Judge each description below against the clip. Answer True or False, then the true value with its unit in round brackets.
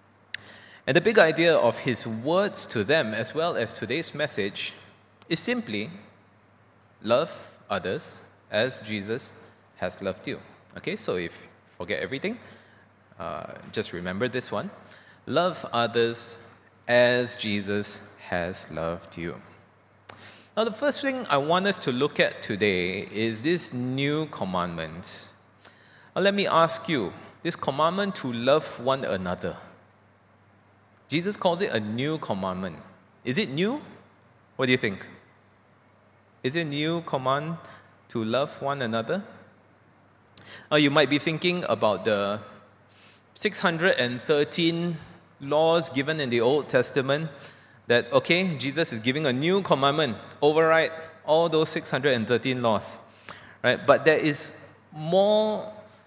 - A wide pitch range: True (7.4 semitones)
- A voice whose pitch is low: True (120 Hz)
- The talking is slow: True (130 wpm)